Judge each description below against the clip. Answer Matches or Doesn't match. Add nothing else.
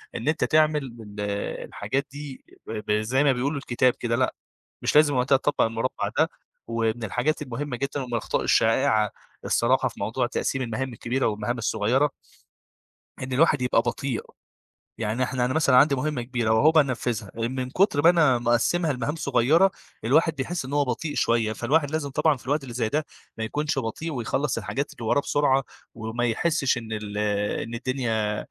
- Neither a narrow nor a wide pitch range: Matches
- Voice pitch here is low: Matches